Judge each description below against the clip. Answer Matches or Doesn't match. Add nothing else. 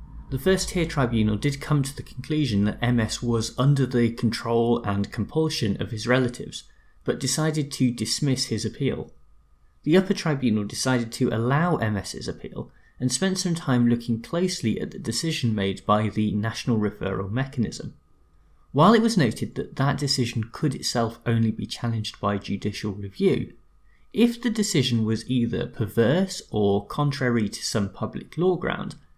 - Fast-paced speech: Doesn't match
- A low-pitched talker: Matches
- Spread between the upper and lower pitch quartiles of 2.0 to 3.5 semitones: Doesn't match